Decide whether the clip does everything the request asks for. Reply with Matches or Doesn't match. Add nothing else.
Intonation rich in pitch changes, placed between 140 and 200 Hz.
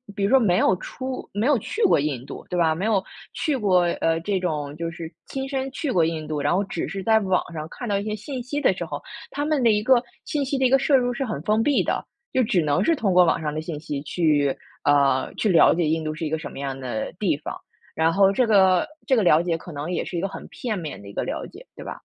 Matches